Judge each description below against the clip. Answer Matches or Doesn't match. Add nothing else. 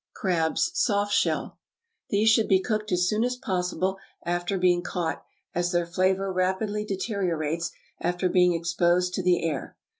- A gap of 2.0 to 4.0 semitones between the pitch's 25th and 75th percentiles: Matches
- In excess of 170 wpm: Doesn't match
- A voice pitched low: Doesn't match